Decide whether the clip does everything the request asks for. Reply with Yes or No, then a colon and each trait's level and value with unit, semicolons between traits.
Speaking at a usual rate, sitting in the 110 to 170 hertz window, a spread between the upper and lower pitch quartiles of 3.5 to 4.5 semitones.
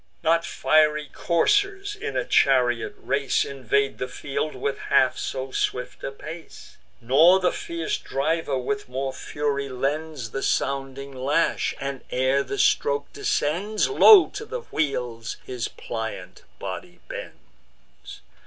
No: slow, 130 wpm; medium, 140 Hz; average, 4.1 semitones